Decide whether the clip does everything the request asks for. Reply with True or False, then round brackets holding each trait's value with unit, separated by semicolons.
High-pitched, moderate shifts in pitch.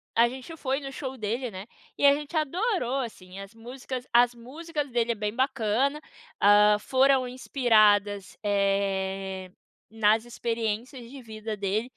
True (235 Hz; 4.2 semitones)